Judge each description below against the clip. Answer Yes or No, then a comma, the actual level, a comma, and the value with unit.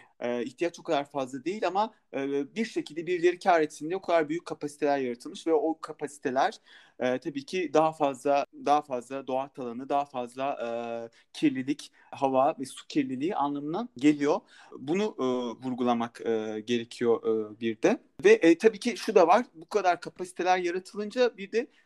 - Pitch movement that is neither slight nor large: No, wide, 7.3 semitones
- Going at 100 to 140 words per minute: No, fast, 150 wpm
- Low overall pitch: No, medium, 150 Hz